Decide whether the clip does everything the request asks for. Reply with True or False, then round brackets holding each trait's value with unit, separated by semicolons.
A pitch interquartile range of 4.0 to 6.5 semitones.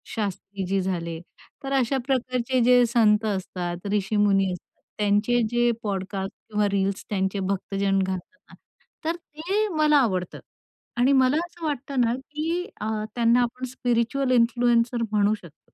True (4.6 semitones)